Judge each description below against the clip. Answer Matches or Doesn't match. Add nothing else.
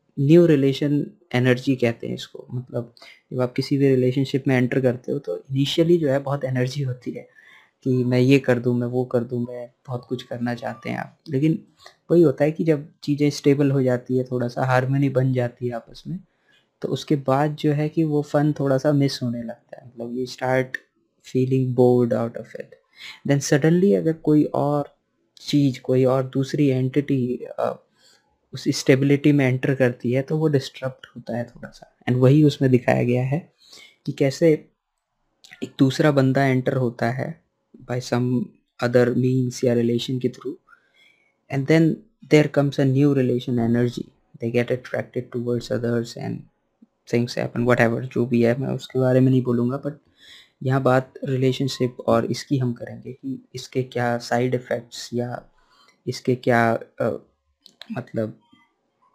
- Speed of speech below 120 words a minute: Doesn't match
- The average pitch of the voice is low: Matches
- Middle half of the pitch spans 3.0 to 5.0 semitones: Doesn't match